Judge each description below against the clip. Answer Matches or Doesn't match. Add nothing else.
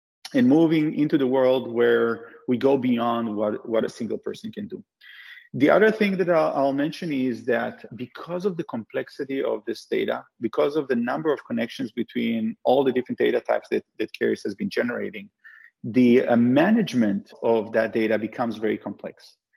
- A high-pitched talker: Doesn't match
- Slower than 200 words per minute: Matches